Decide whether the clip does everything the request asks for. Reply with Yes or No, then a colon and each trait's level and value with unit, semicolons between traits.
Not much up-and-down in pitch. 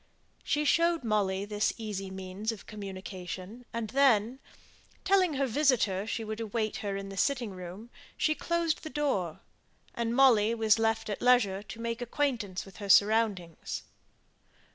No: average, 4.1 semitones